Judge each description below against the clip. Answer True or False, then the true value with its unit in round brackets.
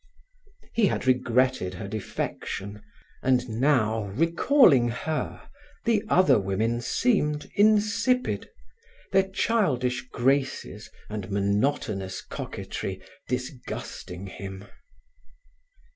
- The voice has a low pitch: True (125 Hz)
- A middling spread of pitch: False (8.1 semitones)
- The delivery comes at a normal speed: False (85 wpm)